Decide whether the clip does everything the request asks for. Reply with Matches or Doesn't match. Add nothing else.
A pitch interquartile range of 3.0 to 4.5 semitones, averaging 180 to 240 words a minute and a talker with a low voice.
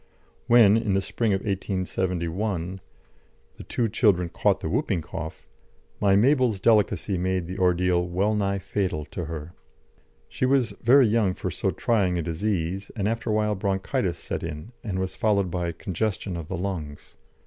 Doesn't match